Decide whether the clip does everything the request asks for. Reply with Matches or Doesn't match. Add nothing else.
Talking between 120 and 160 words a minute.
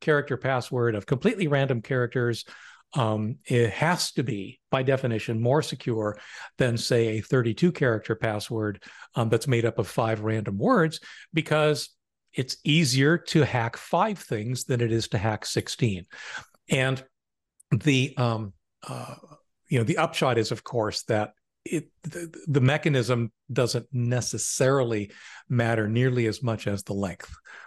Matches